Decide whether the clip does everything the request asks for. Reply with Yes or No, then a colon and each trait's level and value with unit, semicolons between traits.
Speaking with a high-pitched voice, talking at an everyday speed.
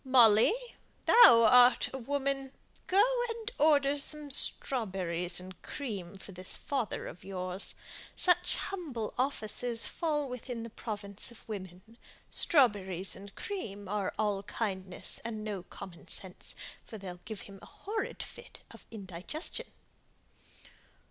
No: high, 220 Hz; slow, 130 wpm